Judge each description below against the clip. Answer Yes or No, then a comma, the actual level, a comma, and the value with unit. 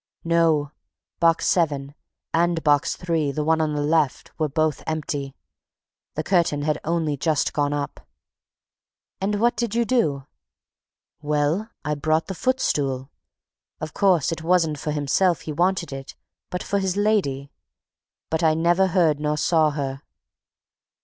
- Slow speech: No, average, 150 wpm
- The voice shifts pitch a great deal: No, average, 3.0 semitones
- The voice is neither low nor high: Yes, medium, 155 Hz